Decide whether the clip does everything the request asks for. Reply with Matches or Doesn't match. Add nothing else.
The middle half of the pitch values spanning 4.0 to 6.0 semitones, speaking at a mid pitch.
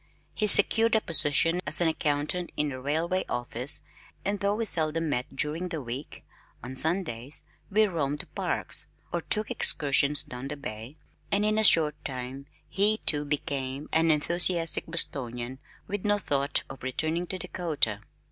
Matches